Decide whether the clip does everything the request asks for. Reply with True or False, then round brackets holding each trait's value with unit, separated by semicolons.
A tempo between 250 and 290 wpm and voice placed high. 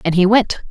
True (255 wpm; 200 Hz)